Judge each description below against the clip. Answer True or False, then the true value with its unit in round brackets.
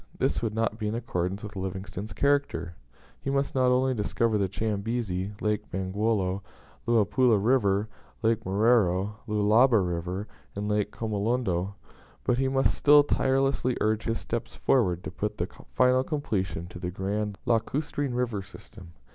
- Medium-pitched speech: False (105 Hz)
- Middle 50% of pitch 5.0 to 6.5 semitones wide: False (4.1 semitones)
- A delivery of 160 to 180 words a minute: False (145 wpm)